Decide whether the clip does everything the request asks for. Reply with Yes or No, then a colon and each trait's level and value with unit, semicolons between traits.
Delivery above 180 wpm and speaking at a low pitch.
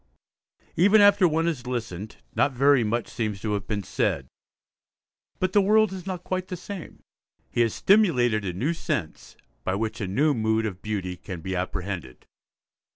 No: average, 170 wpm; low, 120 Hz